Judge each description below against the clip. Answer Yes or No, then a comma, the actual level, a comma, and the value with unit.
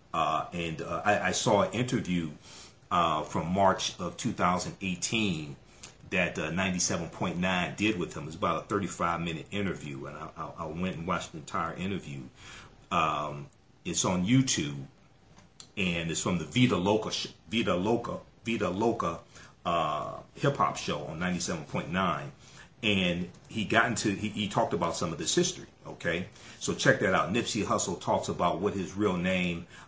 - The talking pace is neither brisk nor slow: Yes, average, 160 wpm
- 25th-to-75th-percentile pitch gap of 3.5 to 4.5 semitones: Yes, average, 4.1 semitones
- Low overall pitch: Yes, very low, 90 Hz